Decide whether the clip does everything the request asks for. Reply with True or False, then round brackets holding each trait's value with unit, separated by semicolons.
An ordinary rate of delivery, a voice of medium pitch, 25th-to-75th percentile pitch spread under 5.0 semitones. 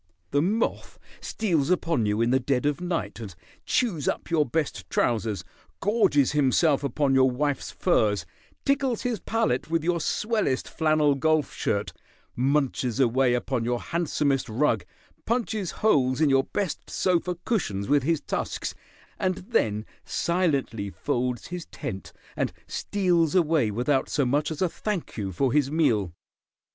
False (150 wpm; 145 Hz; 5.6 semitones)